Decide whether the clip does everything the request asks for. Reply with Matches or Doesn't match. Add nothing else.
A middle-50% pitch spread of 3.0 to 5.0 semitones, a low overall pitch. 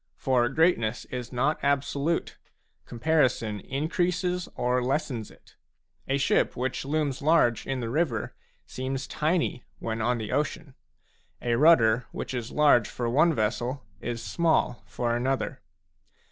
Matches